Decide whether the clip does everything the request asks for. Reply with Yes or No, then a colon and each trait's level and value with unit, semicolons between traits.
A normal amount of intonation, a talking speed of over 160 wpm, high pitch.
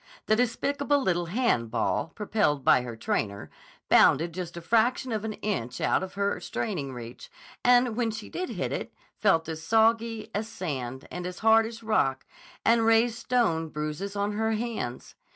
No: wide, 6.0 semitones; average, 170 wpm; high, 210 Hz